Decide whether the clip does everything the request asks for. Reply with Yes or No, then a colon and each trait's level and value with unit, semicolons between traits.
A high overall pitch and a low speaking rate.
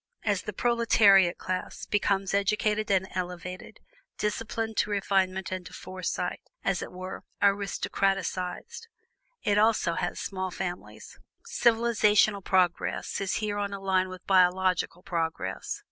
Yes: high, 195 Hz; slow, 125 wpm